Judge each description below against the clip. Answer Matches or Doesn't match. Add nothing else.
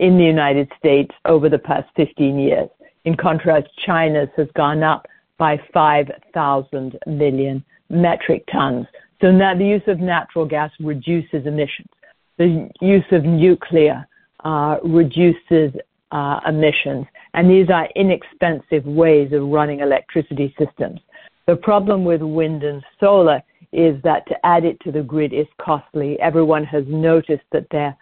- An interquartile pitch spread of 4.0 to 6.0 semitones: Doesn't match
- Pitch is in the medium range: Matches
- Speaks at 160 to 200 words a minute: Doesn't match